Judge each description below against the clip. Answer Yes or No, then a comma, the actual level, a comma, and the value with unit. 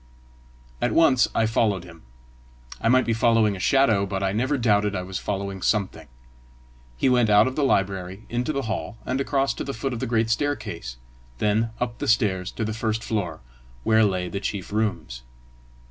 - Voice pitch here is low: Yes, low, 110 Hz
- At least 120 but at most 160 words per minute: No, average, 190 wpm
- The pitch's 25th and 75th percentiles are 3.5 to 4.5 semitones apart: Yes, average, 3.8 semitones